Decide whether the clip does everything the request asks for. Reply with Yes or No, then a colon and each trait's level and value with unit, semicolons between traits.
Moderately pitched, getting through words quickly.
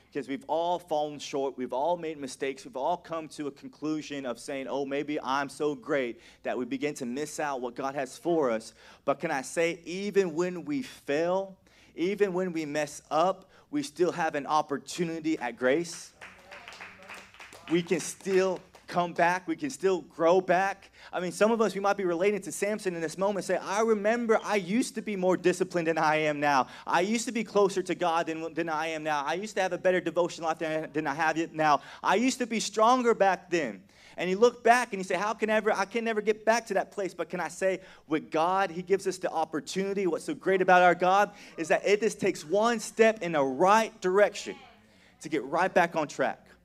Yes: medium, 175 Hz; fast, 225 wpm